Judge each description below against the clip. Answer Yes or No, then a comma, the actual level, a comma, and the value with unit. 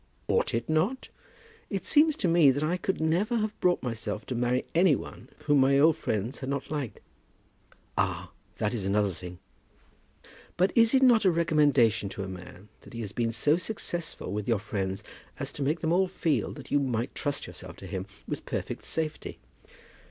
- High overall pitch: No, medium, 140 Hz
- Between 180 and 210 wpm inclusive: Yes, average, 190 wpm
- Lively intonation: Yes, wide, 7.4 semitones